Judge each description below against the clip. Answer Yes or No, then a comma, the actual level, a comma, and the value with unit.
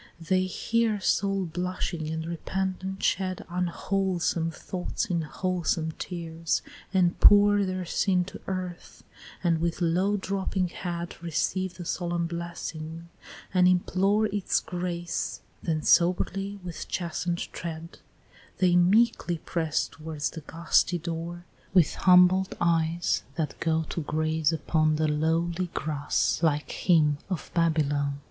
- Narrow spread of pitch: Yes, narrow, 2.3 semitones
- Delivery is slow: Yes, slow, 125 wpm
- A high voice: No, medium, 175 Hz